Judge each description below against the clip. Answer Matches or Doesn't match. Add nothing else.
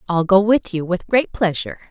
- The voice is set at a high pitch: Matches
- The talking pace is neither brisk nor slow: Doesn't match